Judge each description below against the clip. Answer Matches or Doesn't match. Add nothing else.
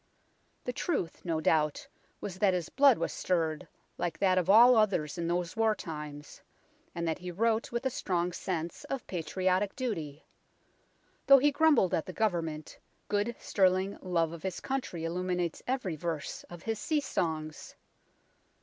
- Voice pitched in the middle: Matches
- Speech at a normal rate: Matches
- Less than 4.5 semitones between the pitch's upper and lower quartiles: Doesn't match